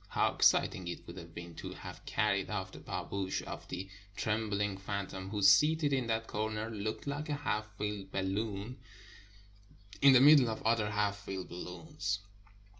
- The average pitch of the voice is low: Yes, low, 105 Hz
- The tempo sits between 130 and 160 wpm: No, average, 170 wpm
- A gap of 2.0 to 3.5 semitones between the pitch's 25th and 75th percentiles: Yes, average, 2.7 semitones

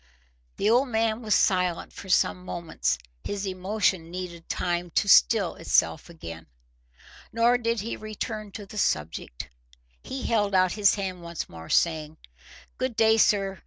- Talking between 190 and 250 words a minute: No, average, 150 wpm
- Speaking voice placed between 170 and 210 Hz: Yes, high, 190 Hz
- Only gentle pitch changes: No, average, 4.3 semitones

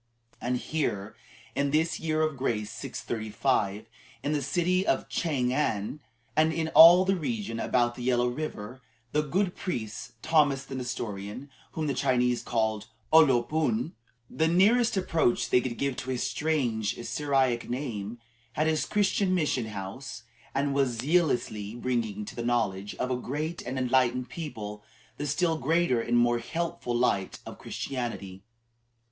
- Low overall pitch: Yes, low, 130 Hz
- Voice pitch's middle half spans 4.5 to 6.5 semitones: Yes, average, 4.8 semitones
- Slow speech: No, average, 155 wpm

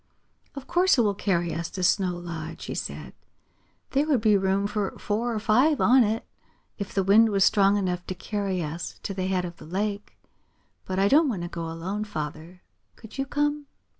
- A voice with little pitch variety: No, average, 3.7 semitones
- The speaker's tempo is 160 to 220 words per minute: Yes, average, 200 wpm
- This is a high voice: Yes, high, 200 Hz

